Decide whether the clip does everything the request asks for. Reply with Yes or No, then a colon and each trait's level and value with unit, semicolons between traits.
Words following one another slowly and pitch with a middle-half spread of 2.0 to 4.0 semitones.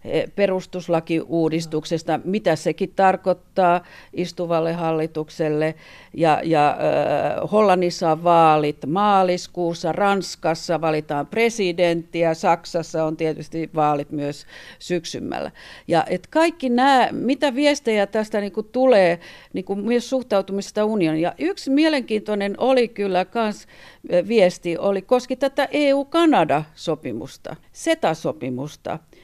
No: slow, 90 wpm; average, 5.1 semitones